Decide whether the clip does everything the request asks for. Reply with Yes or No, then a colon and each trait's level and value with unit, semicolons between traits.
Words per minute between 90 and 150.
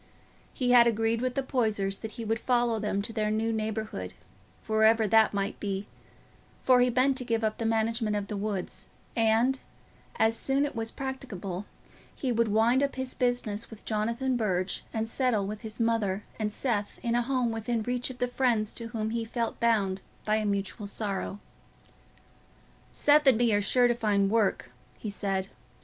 No: average, 185 wpm